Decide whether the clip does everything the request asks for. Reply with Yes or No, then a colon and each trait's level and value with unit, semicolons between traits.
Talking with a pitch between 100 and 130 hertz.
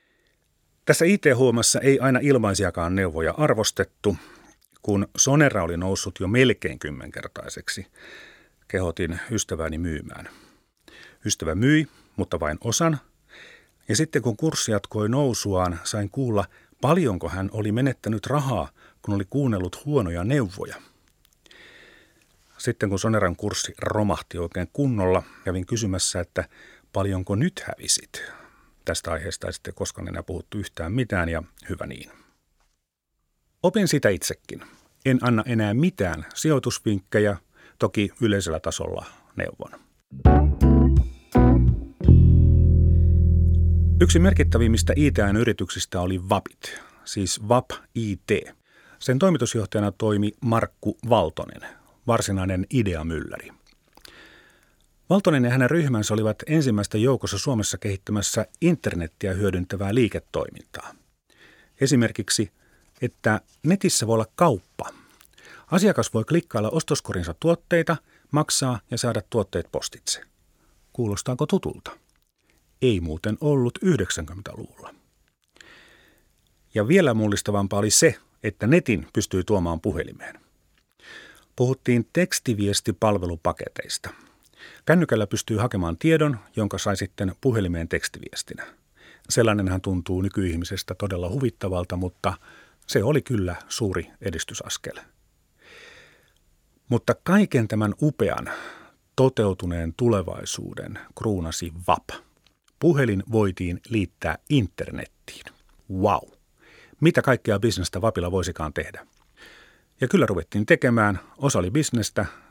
Yes: low, 105 Hz